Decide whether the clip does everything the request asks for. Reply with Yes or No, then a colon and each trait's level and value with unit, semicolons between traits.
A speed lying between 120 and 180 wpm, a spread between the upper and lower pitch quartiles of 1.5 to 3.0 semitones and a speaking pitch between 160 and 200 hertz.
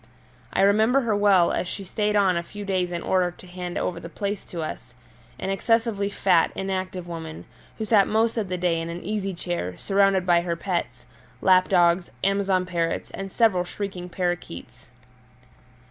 Yes: average, 175 wpm; narrow, 2.5 semitones; medium, 185 Hz